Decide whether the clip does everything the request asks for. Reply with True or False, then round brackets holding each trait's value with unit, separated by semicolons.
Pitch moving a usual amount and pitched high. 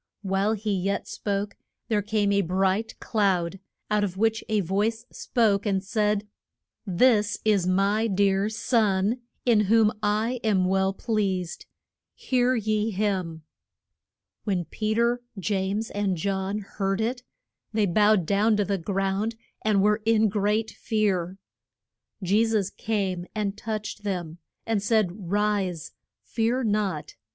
False (2.1 semitones; 205 Hz)